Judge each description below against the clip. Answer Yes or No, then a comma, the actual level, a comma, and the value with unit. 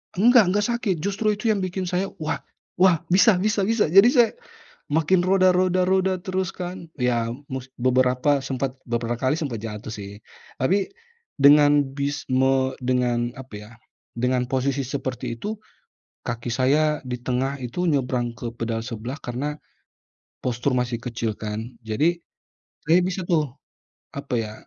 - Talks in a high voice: No, medium, 140 Hz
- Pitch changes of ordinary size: No, wide, 6.8 semitones